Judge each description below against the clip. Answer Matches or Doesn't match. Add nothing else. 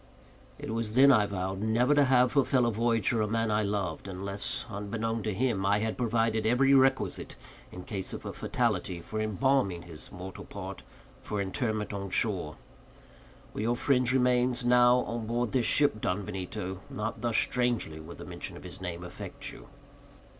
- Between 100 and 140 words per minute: Doesn't match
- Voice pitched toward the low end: Matches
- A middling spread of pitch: Matches